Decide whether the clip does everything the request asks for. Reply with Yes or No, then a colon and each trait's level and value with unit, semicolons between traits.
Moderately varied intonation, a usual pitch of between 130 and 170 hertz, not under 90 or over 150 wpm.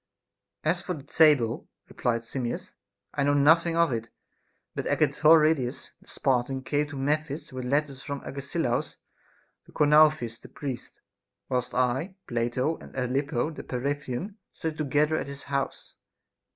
Yes: average, 3.4 semitones; medium, 140 Hz; average, 140 wpm